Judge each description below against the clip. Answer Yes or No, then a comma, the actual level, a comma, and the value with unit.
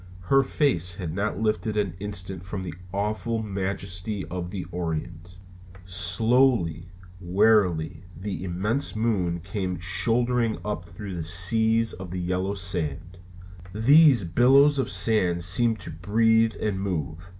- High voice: No, very low, 95 Hz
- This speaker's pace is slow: Yes, slow, 130 wpm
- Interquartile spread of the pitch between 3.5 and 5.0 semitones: Yes, average, 3.9 semitones